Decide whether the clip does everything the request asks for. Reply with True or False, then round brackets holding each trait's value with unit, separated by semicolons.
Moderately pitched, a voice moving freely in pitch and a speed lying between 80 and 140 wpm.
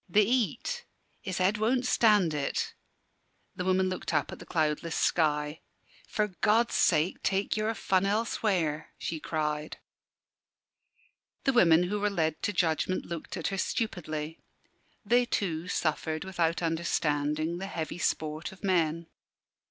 False (175 Hz; 4.6 semitones; 135 wpm)